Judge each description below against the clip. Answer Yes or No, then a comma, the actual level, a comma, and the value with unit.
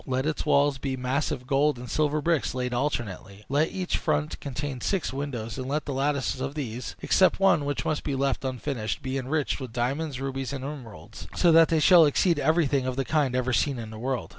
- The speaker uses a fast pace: Yes, fast, 215 wpm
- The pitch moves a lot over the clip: No, average, 2.8 semitones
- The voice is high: No, low, 135 Hz